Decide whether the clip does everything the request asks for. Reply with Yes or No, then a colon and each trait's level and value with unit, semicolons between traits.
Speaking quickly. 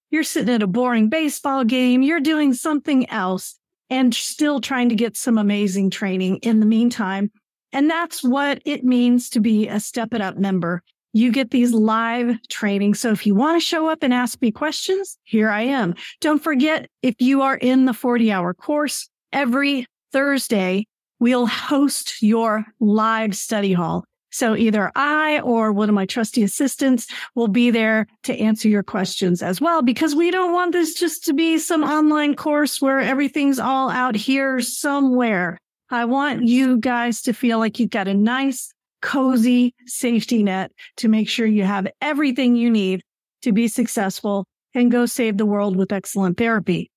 No: average, 180 wpm